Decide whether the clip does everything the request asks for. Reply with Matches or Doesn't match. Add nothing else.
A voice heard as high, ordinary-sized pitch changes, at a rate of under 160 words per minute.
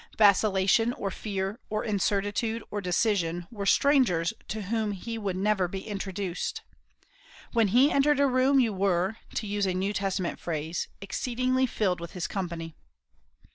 Matches